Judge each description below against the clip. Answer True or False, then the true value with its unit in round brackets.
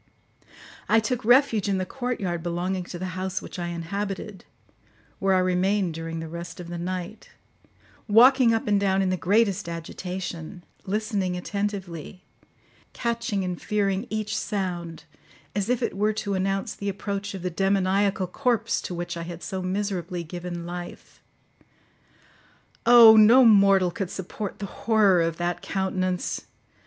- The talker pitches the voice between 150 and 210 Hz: True (190 Hz)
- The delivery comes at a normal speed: True (150 wpm)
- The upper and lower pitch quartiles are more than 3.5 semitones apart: False (2.9 semitones)